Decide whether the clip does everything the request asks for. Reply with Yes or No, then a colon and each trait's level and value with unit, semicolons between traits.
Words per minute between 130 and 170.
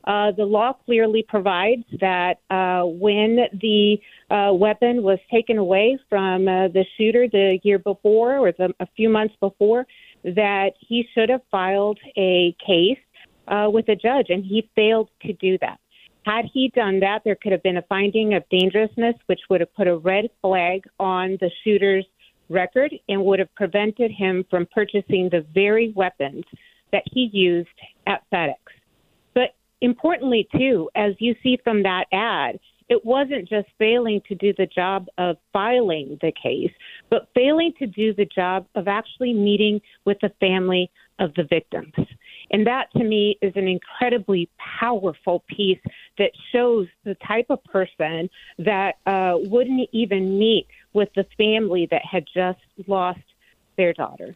Yes: average, 160 wpm